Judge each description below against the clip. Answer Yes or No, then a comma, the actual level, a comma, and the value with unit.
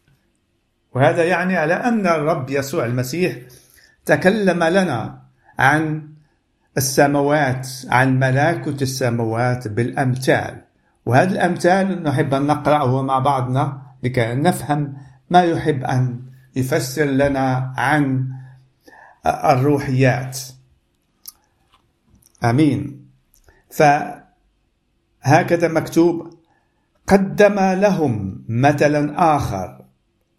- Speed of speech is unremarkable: Yes, average, 75 wpm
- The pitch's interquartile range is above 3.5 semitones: Yes, average, 4.1 semitones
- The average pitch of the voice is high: No, medium, 140 Hz